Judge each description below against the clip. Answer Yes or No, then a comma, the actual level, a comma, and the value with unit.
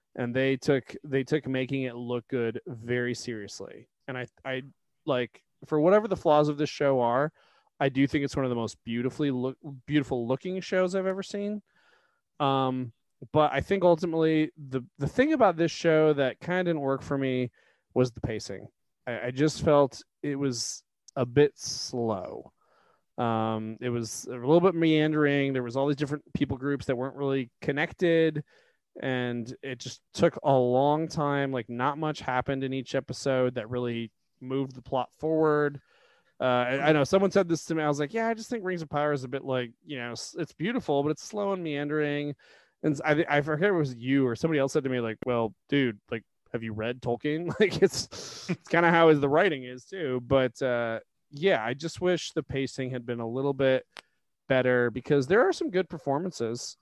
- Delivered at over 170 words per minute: Yes, average, 200 wpm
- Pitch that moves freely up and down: No, average, 3.5 semitones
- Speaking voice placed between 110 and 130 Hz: No, medium, 140 Hz